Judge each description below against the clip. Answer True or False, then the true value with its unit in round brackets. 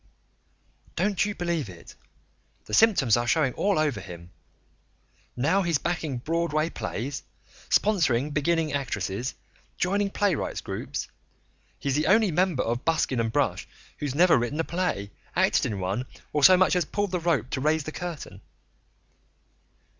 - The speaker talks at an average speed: True (145 wpm)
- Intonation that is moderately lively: False (6.3 semitones)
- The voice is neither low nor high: True (155 Hz)